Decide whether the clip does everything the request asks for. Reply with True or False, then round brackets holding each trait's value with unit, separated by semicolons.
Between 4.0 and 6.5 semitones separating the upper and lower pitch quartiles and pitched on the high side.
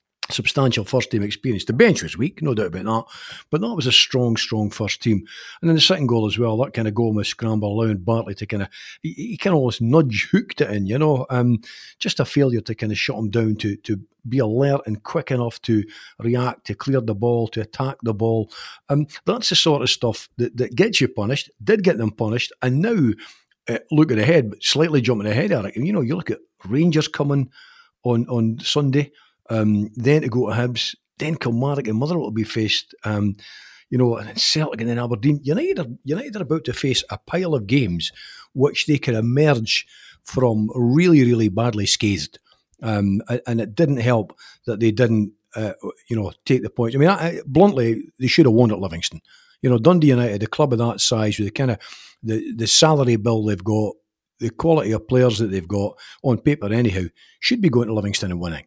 False (4.5 semitones; 120 Hz)